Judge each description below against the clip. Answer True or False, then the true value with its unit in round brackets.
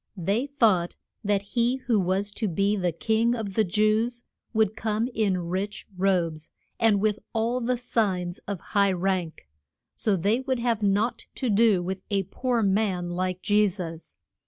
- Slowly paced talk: False (165 wpm)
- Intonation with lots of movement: False (3.4 semitones)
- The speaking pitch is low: False (205 Hz)